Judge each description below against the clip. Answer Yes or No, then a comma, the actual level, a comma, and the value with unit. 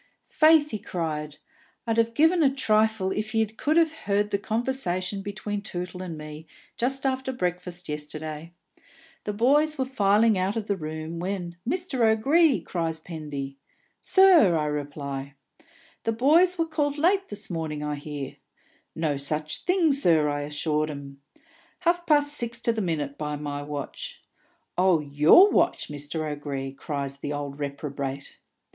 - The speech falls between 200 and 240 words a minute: No, average, 150 wpm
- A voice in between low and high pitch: Yes, medium, 180 Hz